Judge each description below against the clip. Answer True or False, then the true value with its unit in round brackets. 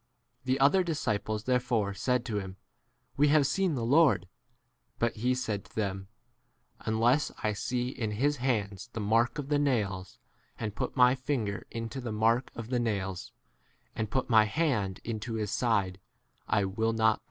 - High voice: False (115 Hz)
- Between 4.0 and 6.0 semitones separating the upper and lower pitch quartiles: False (3.5 semitones)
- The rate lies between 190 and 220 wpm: False (175 wpm)